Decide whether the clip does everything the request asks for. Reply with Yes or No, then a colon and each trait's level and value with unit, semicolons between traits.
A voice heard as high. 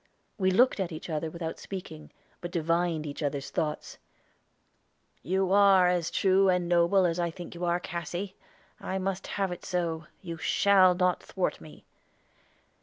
No: medium, 175 Hz